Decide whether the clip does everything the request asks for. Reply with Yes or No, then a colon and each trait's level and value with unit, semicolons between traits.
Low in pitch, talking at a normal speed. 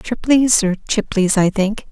No: high, 210 Hz; average, 155 wpm